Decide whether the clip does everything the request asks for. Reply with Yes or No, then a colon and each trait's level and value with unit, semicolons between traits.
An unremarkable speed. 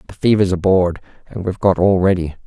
Yes: average, 195 wpm